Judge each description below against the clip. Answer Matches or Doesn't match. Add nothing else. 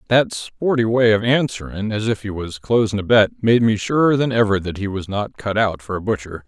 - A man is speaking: Matches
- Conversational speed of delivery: Doesn't match